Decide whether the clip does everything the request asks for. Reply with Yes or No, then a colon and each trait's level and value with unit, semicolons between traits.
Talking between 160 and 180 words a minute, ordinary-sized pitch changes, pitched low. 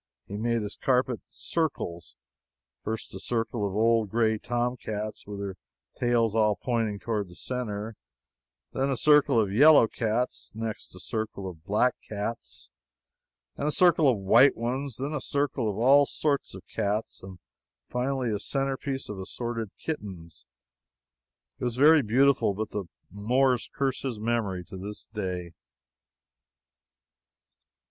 No: average, 145 wpm; average, 4.1 semitones; low, 115 Hz